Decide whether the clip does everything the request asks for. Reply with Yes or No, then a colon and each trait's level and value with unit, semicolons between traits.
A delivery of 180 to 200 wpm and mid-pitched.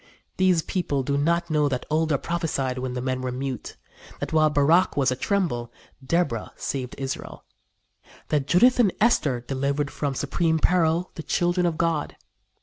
No: average, 155 wpm; medium, 150 Hz